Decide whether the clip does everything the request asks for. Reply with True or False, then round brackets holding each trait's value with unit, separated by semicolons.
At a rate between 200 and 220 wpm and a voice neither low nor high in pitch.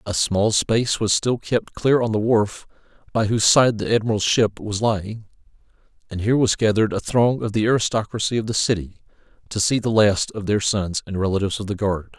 False (205 wpm; 105 Hz)